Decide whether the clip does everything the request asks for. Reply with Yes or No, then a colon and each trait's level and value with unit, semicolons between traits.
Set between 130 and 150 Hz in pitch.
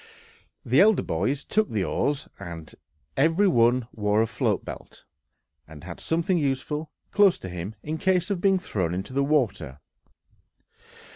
Yes: low, 135 Hz